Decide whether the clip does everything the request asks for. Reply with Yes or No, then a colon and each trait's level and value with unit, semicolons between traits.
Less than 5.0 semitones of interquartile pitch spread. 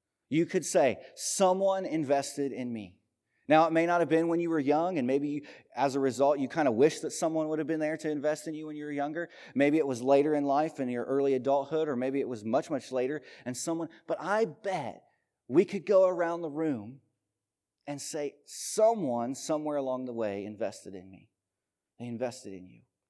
Yes: average, 4.3 semitones